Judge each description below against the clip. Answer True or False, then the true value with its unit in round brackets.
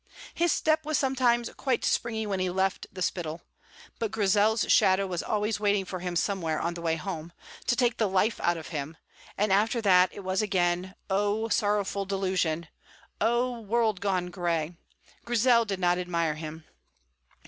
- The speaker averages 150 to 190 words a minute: True (170 wpm)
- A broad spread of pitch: False (3.9 semitones)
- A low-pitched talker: False (195 Hz)